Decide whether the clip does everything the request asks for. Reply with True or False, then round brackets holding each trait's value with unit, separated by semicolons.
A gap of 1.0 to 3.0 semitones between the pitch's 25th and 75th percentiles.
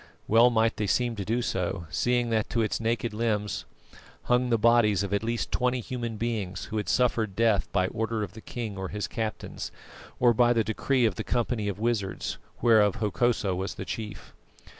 True (2.4 semitones)